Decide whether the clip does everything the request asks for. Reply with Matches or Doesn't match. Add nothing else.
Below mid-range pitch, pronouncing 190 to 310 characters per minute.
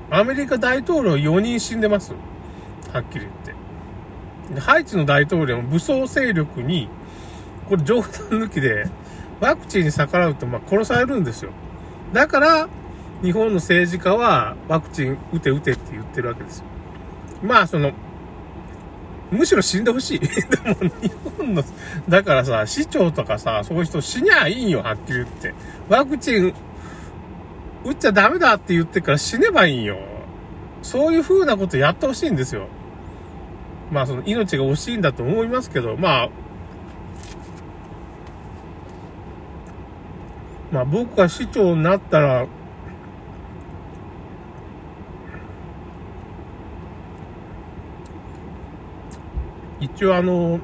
Matches